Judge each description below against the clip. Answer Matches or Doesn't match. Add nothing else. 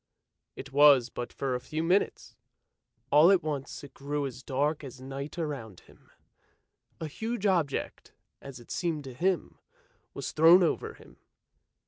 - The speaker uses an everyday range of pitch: Matches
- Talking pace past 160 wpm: Doesn't match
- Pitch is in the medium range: Matches